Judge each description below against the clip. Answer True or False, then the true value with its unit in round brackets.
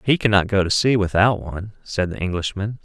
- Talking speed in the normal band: False (210 wpm)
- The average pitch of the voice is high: False (100 Hz)